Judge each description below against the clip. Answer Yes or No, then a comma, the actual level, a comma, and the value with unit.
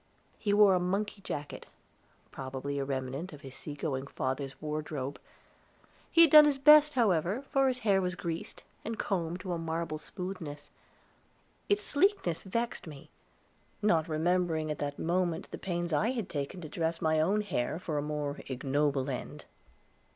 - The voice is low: No, medium, 165 Hz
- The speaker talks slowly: No, average, 165 wpm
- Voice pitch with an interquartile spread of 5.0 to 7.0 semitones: Yes, wide, 5.4 semitones